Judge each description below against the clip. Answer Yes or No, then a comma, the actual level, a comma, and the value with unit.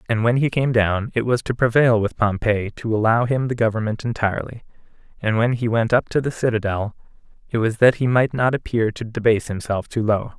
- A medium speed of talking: No, fast, 215 wpm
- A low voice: Yes, low, 115 Hz